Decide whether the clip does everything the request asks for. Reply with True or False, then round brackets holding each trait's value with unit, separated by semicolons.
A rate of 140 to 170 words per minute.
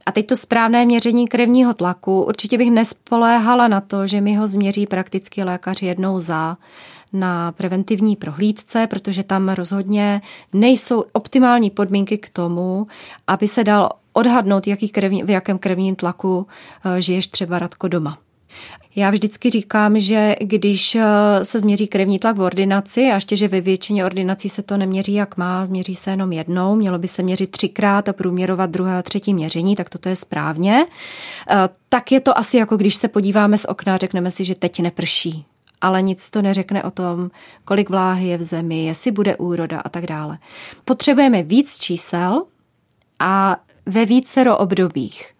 True (165 wpm)